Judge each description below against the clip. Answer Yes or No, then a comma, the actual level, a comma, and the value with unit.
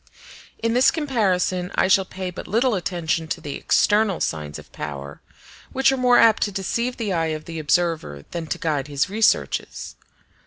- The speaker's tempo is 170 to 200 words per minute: Yes, average, 180 wpm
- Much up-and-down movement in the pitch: Yes, wide, 6.1 semitones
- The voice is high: No, medium, 180 Hz